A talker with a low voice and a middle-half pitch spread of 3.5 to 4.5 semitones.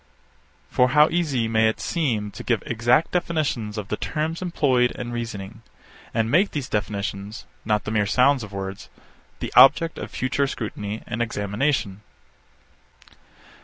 No: low, 115 Hz; average, 5.2 semitones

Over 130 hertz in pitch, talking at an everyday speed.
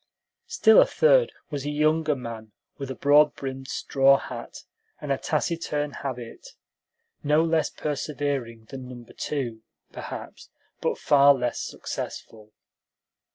No: medium, 140 Hz; slow, 125 wpm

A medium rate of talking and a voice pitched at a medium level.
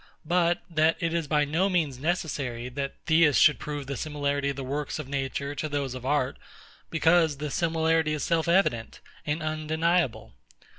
Yes: average, 170 wpm; medium, 150 Hz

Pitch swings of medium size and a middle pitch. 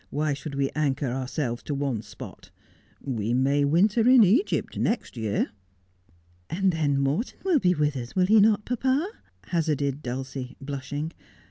No: wide, 6.3 semitones; medium, 145 Hz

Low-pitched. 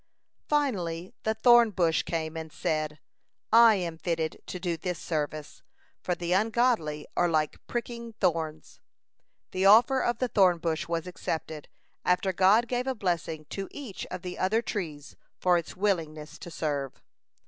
No: medium, 180 Hz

